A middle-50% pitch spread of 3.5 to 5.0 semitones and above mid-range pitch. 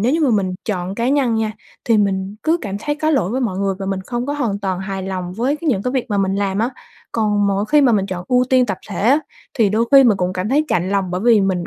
Yes: average, 4.6 semitones; high, 210 Hz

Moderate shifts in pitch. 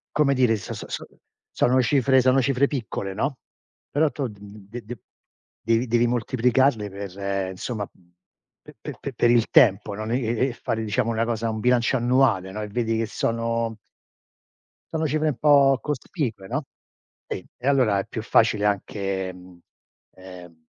Yes: average, 4.0 semitones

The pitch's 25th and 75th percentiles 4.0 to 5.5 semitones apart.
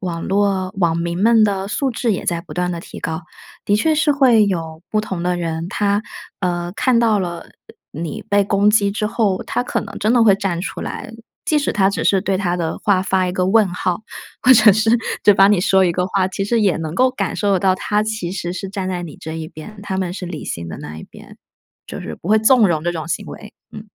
No: average, 3.4 semitones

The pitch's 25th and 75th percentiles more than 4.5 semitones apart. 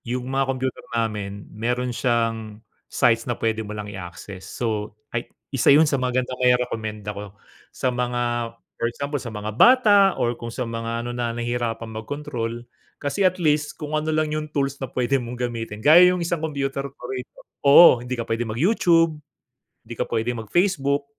No: average, 3.9 semitones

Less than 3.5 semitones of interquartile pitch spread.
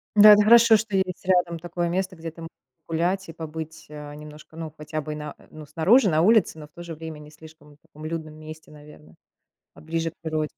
Yes: narrow, 2.6 semitones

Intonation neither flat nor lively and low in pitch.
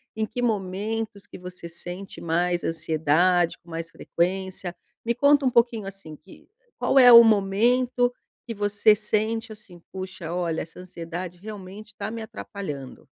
No: average, 3.9 semitones; high, 195 Hz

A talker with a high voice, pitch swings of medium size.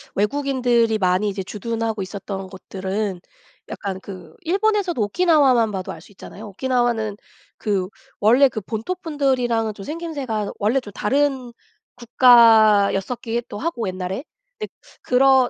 Yes: high, 225 Hz; average, 4.6 semitones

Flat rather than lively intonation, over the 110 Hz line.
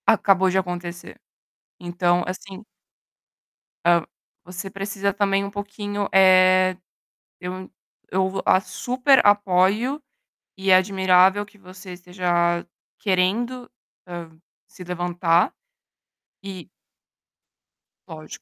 Yes: narrow, 1.9 semitones; medium, 185 Hz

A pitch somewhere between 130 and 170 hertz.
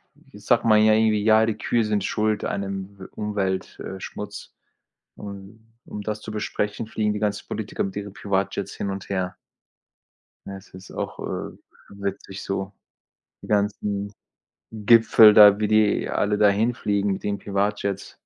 No: low, 105 Hz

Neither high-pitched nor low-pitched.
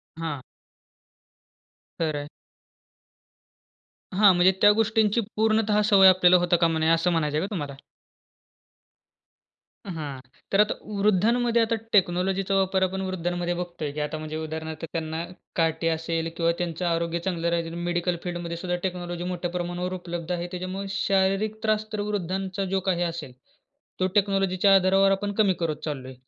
Yes: medium, 180 Hz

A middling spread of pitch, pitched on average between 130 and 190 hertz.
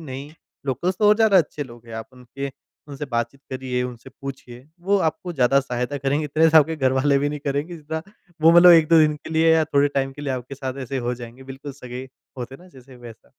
Yes: average, 3.5 semitones; medium, 140 Hz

